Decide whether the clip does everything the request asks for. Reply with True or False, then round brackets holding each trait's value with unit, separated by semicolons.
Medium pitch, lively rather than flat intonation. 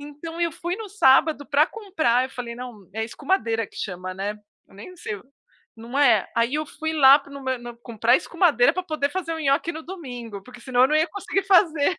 False (280 Hz; 5.7 semitones)